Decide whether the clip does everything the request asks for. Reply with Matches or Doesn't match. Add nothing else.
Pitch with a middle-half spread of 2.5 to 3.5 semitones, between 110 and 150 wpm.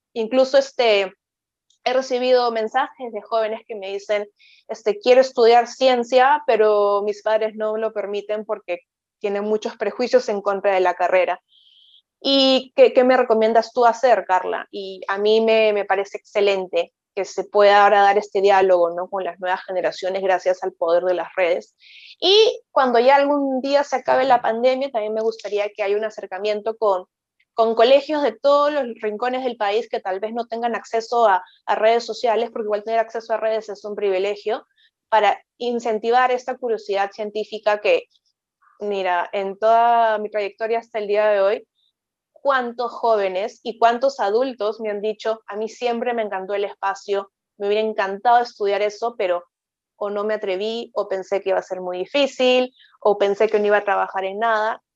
Doesn't match